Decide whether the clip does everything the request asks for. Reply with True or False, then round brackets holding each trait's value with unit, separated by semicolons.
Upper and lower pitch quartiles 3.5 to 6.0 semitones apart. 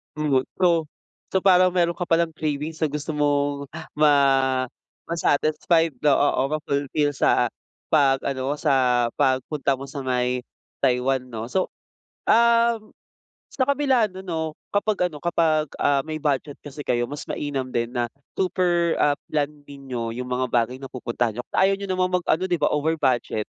True (4.4 semitones)